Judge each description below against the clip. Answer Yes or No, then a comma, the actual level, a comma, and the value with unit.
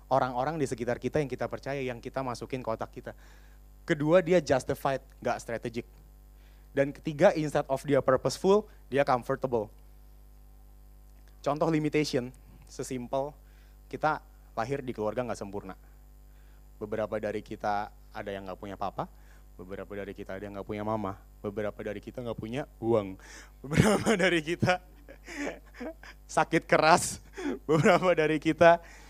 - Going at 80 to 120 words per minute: No, average, 135 wpm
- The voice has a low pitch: Yes, low, 125 Hz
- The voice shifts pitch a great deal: Yes, wide, 6.0 semitones